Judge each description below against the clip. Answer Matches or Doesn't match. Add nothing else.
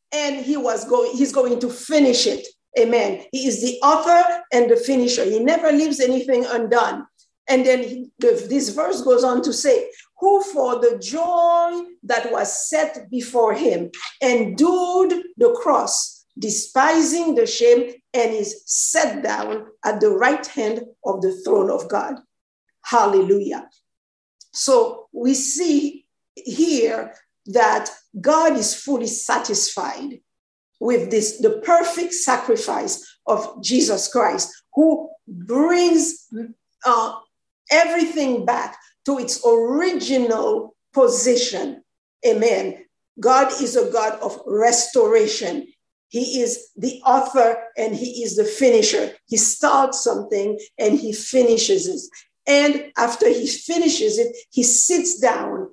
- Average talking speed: Doesn't match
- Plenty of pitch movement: Matches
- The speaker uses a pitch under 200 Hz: Doesn't match